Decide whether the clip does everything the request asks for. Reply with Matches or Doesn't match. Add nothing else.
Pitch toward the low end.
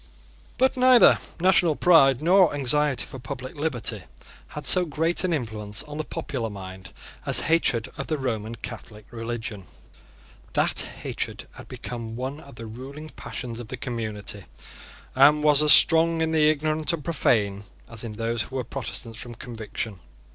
Matches